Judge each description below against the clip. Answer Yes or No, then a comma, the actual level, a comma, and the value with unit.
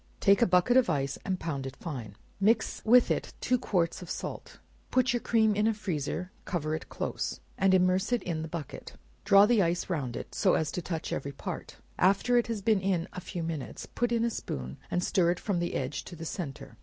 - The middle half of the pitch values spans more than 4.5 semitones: Yes, average, 5.1 semitones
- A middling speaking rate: No, fast, 225 wpm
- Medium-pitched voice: Yes, medium, 180 Hz